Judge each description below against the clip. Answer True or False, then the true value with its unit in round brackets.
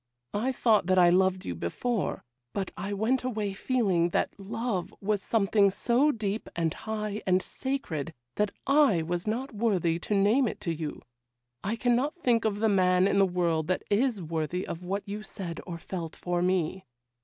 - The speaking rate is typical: True (180 wpm)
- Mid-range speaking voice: False (200 Hz)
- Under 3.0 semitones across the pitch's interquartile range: False (4.1 semitones)